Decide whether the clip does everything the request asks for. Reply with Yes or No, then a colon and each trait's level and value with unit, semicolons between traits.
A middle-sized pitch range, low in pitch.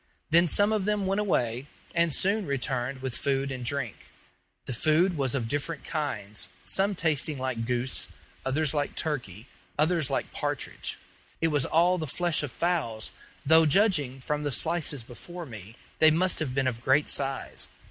No: average, 4.7 semitones; medium, 145 Hz